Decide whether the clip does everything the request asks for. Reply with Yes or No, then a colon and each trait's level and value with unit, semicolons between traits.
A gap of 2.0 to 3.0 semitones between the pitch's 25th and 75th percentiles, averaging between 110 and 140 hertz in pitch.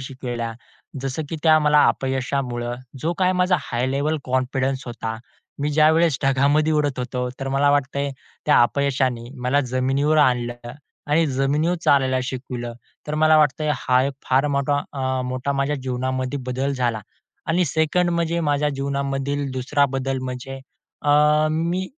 Yes: narrow, 2.5 semitones; low, 135 Hz